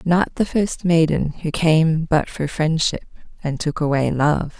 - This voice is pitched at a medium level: Yes, medium, 160 Hz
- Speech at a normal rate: Yes, average, 170 wpm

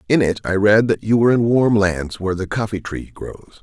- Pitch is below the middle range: Yes, low, 105 Hz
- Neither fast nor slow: No, fast, 250 wpm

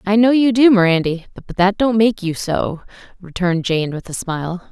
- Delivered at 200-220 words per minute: Yes, fast, 205 wpm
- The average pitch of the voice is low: No, high, 190 Hz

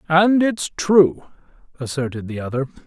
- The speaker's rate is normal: No, slow, 125 wpm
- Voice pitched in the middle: Yes, medium, 155 Hz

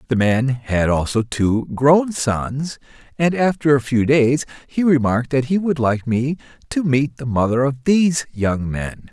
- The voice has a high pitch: No, low, 135 Hz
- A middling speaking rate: Yes, average, 180 wpm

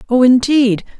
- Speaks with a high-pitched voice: Yes, very high, 250 Hz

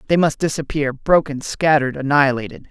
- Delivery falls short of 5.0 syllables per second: No, 6.0 syllables/s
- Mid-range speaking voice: Yes, medium, 145 Hz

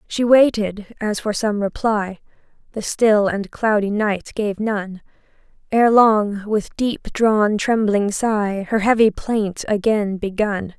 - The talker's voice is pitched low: No, high, 210 Hz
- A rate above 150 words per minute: No, slow, 135 wpm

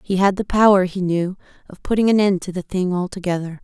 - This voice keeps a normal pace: No, fast, 230 wpm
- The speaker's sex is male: No, female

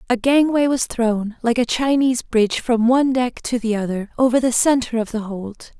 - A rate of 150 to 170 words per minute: No, fast, 205 wpm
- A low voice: No, high, 240 Hz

